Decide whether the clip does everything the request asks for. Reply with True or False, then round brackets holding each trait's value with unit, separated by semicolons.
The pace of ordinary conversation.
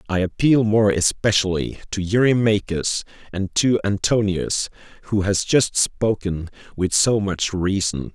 False (125 wpm)